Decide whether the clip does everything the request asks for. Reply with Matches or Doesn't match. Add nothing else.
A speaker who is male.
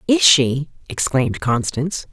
Doesn't match